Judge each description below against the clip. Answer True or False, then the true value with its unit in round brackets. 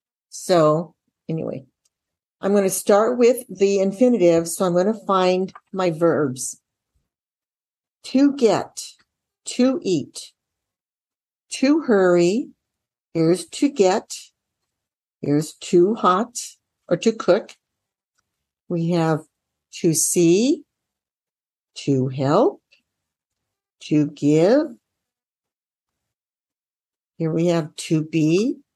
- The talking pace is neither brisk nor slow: False (90 wpm)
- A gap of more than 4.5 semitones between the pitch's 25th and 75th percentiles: True (5.3 semitones)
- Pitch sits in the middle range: True (175 Hz)